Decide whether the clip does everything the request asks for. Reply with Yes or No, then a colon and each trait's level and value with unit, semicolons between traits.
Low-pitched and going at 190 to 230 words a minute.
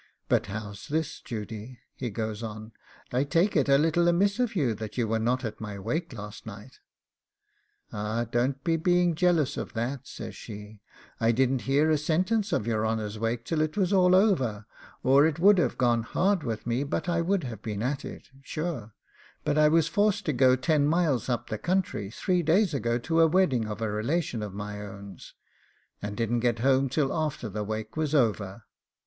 Yes: low, 130 Hz; average, 200 wpm